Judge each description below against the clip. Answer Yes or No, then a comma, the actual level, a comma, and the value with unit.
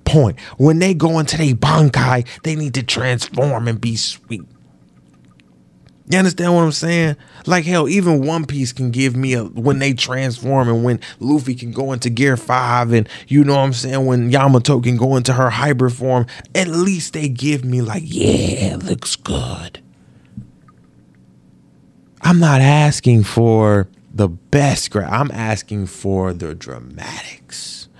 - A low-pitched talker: Yes, low, 130 Hz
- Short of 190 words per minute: Yes, average, 160 wpm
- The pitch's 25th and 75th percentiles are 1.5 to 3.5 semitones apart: No, average, 4.3 semitones